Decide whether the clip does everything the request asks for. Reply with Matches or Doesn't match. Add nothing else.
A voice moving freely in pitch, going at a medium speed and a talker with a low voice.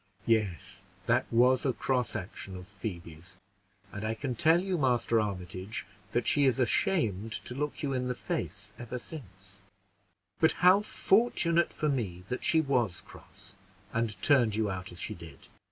Matches